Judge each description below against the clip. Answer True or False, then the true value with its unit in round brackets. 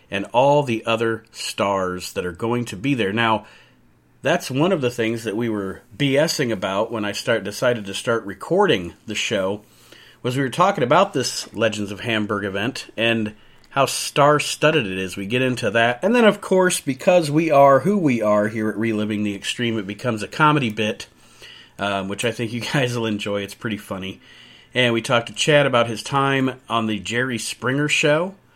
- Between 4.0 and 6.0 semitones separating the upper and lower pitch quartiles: True (4.7 semitones)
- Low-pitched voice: True (115 Hz)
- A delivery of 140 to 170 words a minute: False (200 wpm)